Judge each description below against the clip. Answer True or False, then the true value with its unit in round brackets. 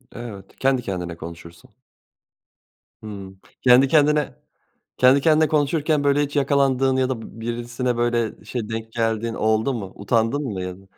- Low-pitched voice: True (120 Hz)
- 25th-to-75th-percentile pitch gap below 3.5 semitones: False (4.1 semitones)